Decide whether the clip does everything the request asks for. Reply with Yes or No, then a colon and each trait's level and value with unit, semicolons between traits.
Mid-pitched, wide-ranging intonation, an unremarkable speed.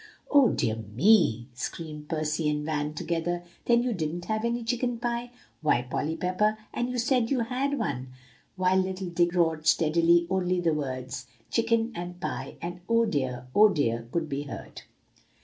Yes: medium, 175 Hz; wide, 7.0 semitones; average, 165 wpm